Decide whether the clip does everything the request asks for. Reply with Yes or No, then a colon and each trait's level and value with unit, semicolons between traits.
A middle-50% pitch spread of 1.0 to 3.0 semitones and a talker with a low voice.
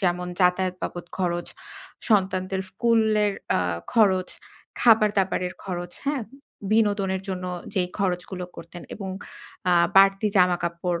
No: narrow, 2.4 semitones; high, 190 Hz